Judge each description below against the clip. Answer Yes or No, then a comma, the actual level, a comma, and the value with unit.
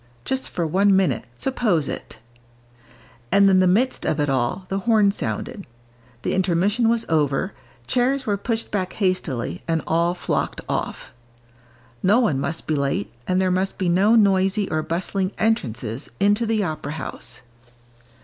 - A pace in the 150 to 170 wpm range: Yes, average, 155 wpm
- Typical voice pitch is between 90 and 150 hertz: No, medium, 185 Hz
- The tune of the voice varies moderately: Yes, average, 4.6 semitones